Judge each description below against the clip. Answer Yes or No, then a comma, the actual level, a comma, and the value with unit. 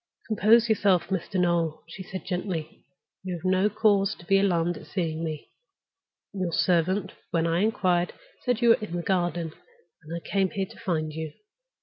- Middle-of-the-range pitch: Yes, medium, 180 Hz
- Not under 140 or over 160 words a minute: No, average, 180 wpm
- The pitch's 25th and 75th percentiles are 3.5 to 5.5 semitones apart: No, average, 2.9 semitones